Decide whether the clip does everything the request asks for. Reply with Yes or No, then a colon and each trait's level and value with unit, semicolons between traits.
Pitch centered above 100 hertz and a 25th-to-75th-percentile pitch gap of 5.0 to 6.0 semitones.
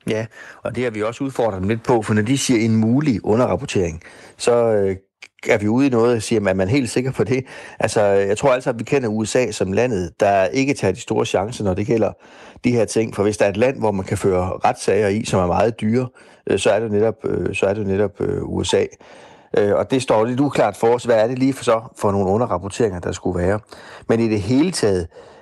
No: low, 110 Hz; average, 3.8 semitones